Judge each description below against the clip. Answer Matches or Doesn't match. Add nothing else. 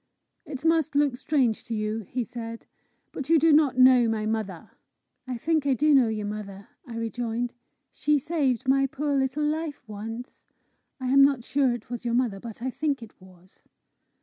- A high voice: Matches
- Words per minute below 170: Doesn't match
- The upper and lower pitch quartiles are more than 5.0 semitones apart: Doesn't match